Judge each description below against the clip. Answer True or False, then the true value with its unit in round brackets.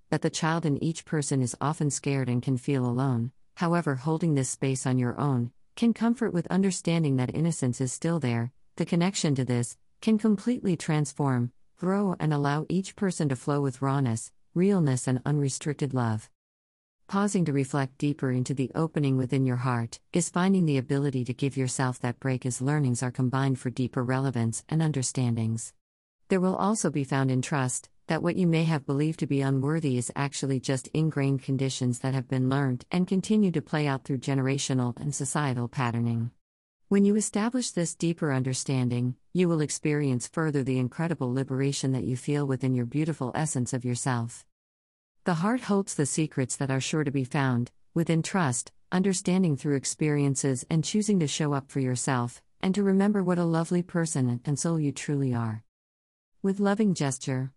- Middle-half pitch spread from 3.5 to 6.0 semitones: True (4.3 semitones)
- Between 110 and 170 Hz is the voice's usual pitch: True (140 Hz)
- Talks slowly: False (180 wpm)